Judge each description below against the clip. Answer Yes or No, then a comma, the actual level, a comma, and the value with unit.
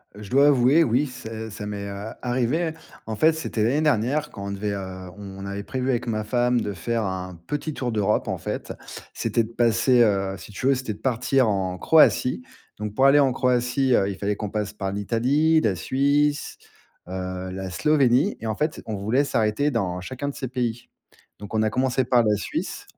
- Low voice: Yes, low, 115 Hz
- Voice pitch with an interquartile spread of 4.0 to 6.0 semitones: Yes, average, 4.7 semitones